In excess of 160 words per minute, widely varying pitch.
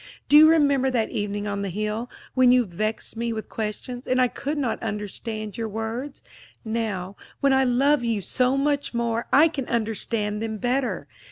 No: average, 180 wpm; average, 3.6 semitones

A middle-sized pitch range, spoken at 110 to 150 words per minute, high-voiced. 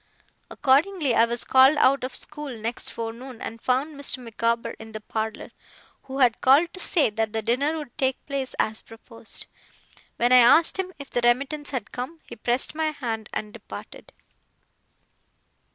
No: average, 3.7 semitones; average, 170 wpm; very high, 255 Hz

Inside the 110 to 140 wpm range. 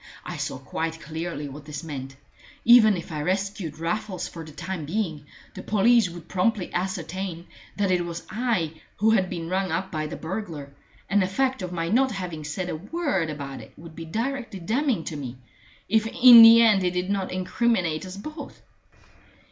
No: average, 190 wpm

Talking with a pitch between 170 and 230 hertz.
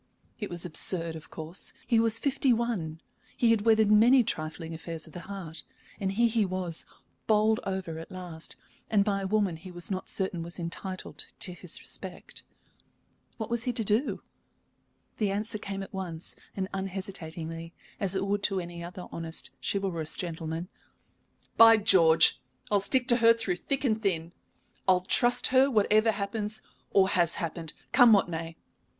Yes: high, 190 Hz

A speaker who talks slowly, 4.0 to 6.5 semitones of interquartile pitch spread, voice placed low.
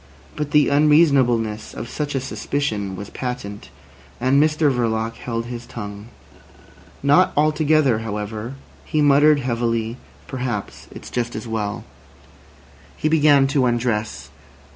Yes: slow, 120 wpm; average, 4.5 semitones; low, 125 Hz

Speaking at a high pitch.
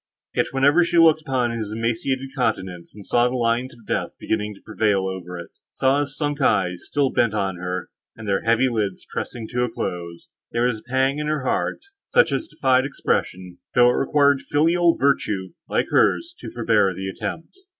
No: low, 120 Hz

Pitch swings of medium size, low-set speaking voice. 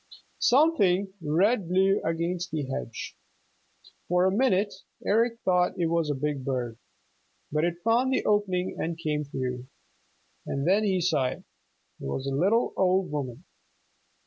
No: average, 5.0 semitones; medium, 180 Hz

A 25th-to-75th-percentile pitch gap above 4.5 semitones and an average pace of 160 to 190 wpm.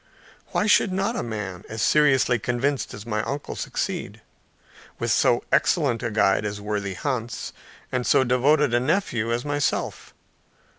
No: average, 5.1 semitones; average, 150 wpm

